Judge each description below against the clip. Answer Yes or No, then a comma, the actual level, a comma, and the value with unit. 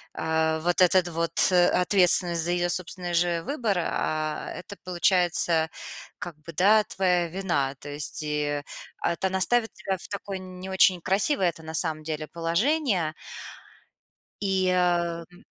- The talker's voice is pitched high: No, medium, 175 Hz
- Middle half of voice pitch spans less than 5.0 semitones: Yes, narrow, 2.5 semitones